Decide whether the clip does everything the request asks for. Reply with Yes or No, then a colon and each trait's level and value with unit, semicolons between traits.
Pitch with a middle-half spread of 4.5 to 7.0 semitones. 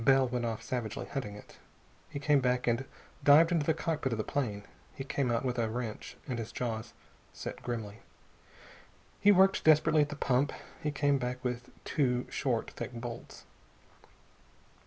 No: average, 3.5 semitones